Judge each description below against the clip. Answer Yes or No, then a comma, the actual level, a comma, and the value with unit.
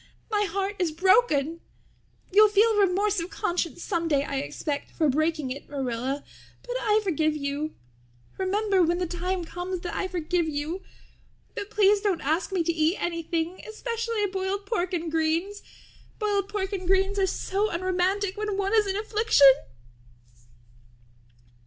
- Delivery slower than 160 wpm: Yes, average, 150 wpm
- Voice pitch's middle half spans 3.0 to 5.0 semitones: Yes, average, 3.9 semitones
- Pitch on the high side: Yes, very high, 370 Hz